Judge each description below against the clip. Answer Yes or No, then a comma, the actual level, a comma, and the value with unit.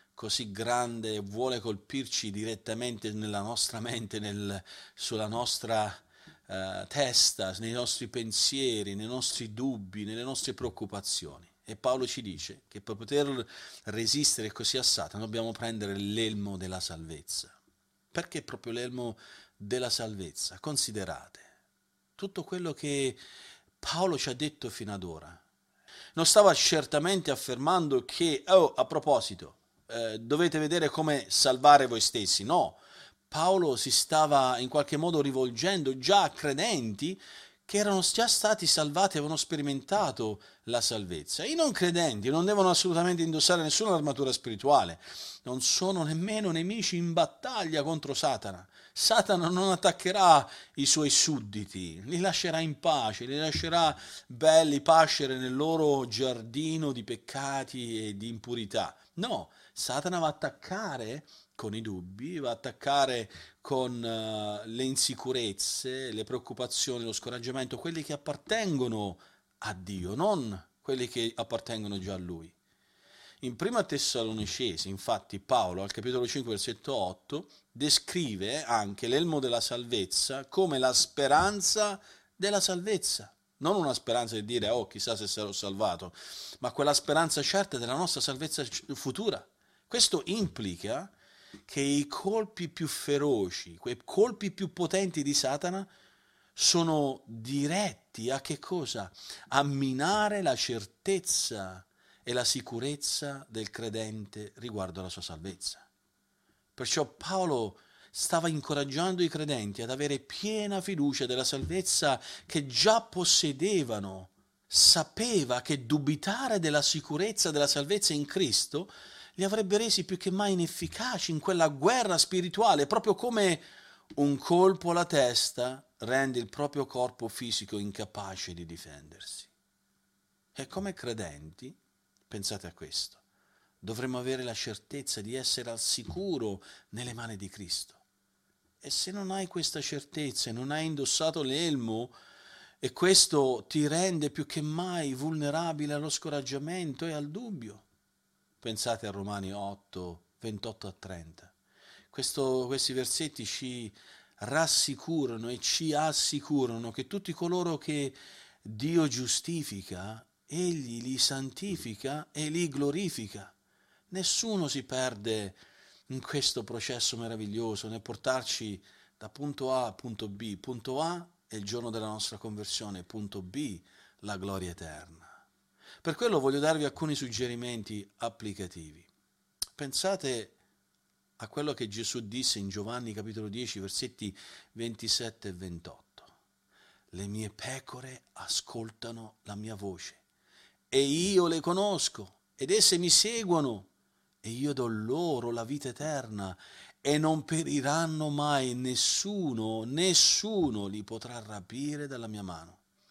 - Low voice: Yes, low, 130 Hz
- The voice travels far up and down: Yes, wide, 6.4 semitones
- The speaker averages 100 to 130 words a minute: Yes, average, 125 wpm